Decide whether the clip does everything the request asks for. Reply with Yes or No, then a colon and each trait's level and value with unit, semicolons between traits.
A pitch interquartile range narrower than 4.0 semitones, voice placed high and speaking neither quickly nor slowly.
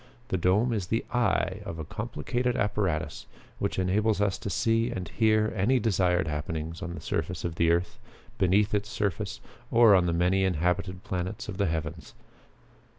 No: average, 3.6 semitones; very low, 95 Hz; average, 170 wpm